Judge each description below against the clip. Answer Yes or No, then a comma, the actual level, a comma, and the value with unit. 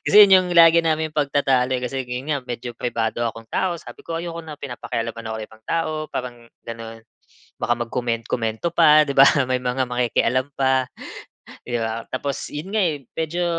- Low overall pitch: Yes, low, 130 Hz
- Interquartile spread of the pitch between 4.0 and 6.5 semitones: Yes, average, 4.8 semitones